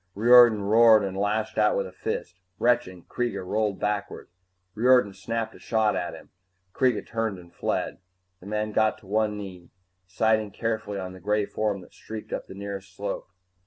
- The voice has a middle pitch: No, low, 105 Hz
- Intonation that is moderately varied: No, narrow, 2.2 semitones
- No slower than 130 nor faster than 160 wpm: No, average, 175 wpm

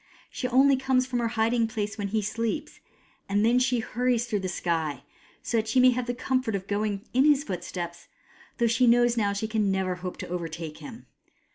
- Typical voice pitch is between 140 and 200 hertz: No, high, 225 Hz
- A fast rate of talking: Yes, fast, 215 wpm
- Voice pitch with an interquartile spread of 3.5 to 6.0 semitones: Yes, average, 3.9 semitones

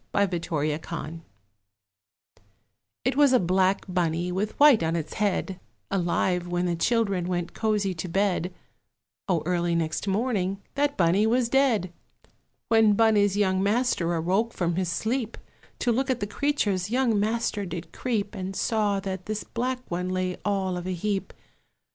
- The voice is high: Yes, high, 195 Hz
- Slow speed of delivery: No, average, 155 wpm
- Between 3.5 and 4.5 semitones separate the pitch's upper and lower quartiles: Yes, average, 3.8 semitones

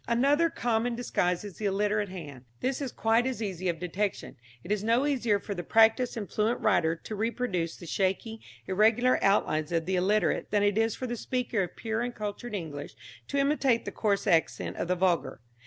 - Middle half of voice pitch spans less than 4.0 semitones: No, average, 4.3 semitones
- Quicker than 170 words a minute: Yes, average, 200 wpm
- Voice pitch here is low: No, high, 210 Hz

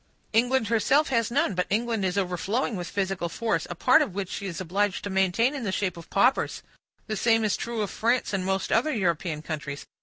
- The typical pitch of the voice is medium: No, high, 200 Hz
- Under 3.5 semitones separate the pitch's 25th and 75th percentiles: No, average, 4.1 semitones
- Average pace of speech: No, fast, 215 wpm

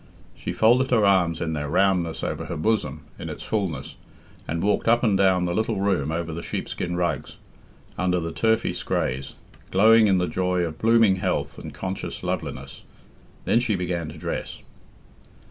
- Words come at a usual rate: Yes, average, 175 wpm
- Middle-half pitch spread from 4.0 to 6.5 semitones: Yes, average, 4.3 semitones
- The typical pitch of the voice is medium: No, very low, 90 Hz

